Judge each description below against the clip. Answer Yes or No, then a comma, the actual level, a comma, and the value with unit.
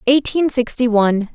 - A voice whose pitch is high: Yes, high, 245 Hz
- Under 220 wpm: Yes, slow, 135 wpm